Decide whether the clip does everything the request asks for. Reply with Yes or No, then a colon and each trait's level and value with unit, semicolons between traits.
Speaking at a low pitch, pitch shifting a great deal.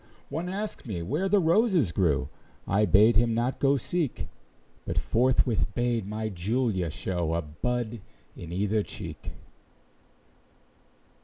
Yes: low, 110 Hz; wide, 6.0 semitones